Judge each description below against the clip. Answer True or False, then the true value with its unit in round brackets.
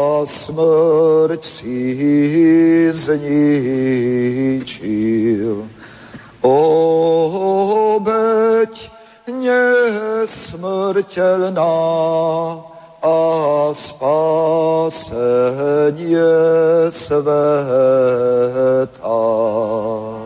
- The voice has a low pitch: False (160 Hz)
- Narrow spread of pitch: False (4.1 semitones)